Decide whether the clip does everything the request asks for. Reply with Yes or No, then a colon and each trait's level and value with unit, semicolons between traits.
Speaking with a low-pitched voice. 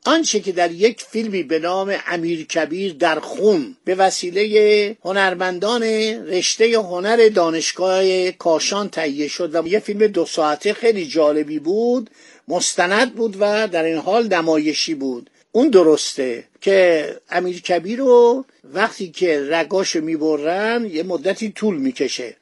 No: medium, 185 Hz